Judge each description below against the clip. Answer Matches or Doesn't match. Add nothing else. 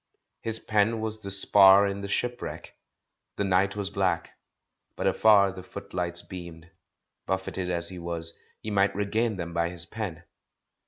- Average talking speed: Matches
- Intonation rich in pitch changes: Doesn't match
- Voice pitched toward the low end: Matches